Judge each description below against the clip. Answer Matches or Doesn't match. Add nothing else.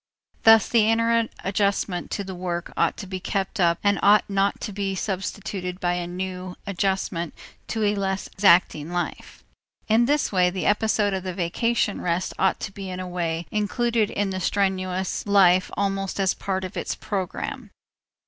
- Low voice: Doesn't match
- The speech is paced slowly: Doesn't match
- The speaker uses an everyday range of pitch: Doesn't match